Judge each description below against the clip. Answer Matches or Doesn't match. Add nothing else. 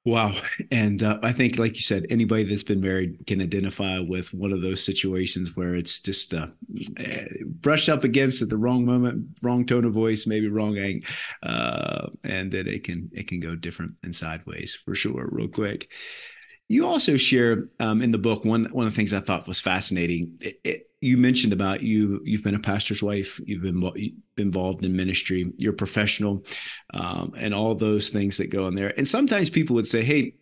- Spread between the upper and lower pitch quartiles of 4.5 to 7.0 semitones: Doesn't match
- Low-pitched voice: Matches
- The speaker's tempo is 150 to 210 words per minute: Matches